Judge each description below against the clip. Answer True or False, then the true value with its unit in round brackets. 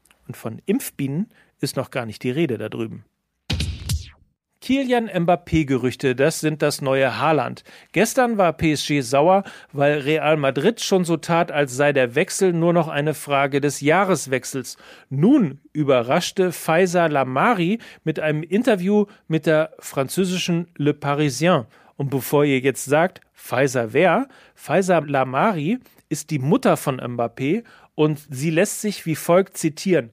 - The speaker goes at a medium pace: True (140 wpm)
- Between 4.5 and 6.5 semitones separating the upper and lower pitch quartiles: True (5.0 semitones)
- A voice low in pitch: False (155 Hz)